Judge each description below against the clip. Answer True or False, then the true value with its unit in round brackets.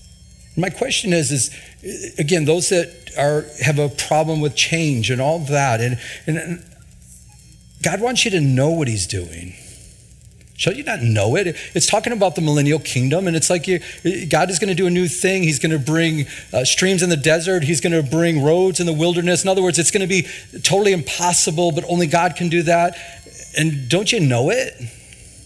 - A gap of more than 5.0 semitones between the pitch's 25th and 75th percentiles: False (3.8 semitones)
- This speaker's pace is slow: False (205 wpm)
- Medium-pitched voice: True (165 Hz)